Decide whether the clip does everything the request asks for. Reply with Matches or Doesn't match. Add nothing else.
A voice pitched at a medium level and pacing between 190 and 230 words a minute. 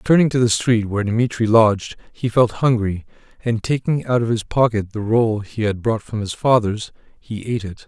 Doesn't match